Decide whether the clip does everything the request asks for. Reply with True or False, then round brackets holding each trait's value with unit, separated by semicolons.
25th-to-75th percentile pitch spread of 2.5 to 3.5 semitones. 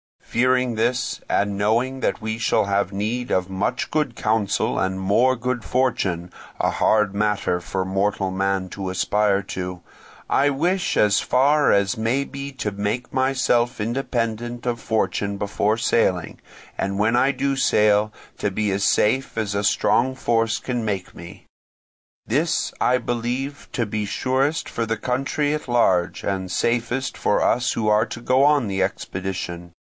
False (4.2 semitones)